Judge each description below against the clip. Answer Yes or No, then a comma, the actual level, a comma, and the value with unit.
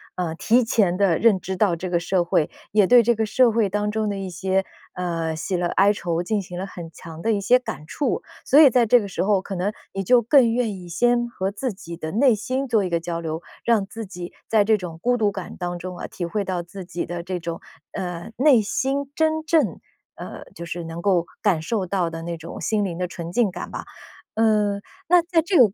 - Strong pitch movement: No, average, 4.5 semitones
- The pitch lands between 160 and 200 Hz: Yes, high, 195 Hz